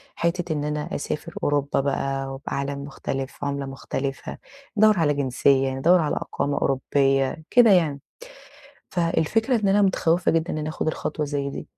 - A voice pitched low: No, medium, 145 Hz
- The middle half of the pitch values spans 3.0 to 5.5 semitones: Yes, average, 3.5 semitones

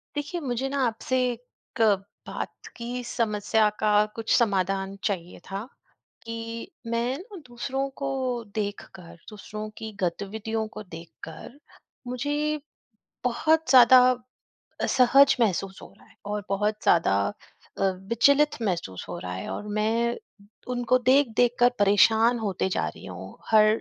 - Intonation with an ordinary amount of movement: Yes, average, 3.7 semitones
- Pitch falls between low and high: No, high, 225 Hz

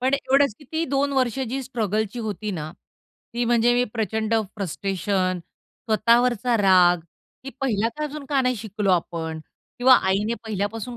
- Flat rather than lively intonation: No, average, 4.1 semitones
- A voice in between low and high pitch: No, high, 225 Hz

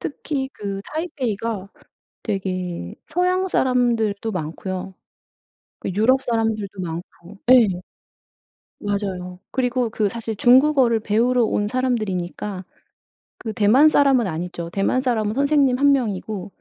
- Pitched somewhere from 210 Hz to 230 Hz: Yes, high, 220 Hz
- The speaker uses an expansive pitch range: No, average, 4.7 semitones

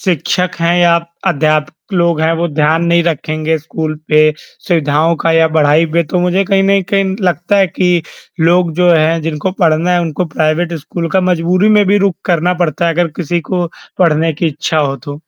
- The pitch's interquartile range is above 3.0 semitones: No, narrow, 2.4 semitones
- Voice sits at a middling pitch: Yes, medium, 170 Hz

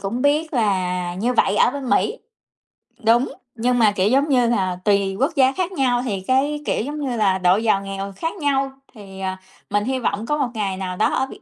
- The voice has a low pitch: No, high, 230 Hz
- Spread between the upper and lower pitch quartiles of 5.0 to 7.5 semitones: Yes, wide, 5.5 semitones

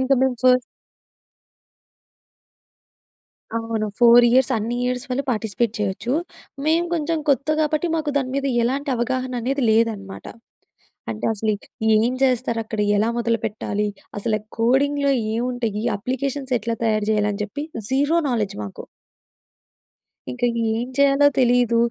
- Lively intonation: No, average, 3.4 semitones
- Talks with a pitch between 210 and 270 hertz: Yes, high, 240 Hz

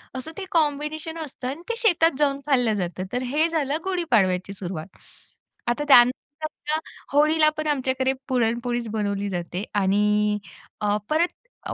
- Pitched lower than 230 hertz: No, very high, 260 Hz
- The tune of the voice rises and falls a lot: Yes, wide, 6.8 semitones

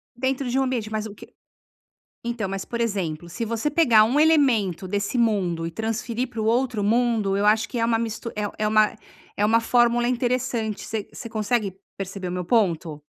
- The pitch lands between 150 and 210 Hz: No, high, 220 Hz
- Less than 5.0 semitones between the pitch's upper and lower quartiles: Yes, average, 3.0 semitones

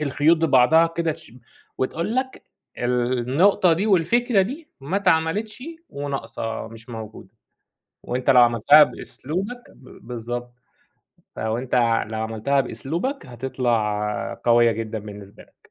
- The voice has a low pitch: Yes, low, 130 Hz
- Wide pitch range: Yes, wide, 6.2 semitones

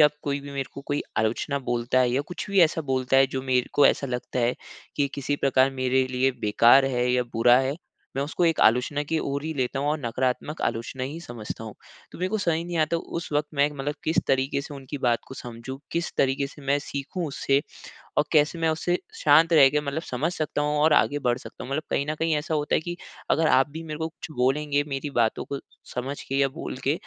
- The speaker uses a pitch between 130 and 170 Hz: Yes, medium, 140 Hz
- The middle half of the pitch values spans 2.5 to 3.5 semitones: Yes, average, 2.8 semitones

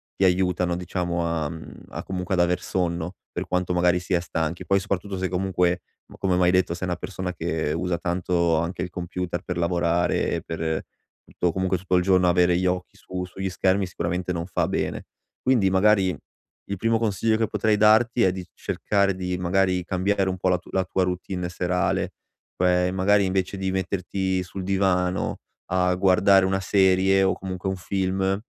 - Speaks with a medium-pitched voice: No, very low, 90 Hz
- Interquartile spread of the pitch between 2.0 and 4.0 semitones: No, narrow, 1.3 semitones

